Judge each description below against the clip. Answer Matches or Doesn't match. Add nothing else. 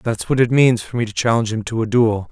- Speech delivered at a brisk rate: Matches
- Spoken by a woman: Doesn't match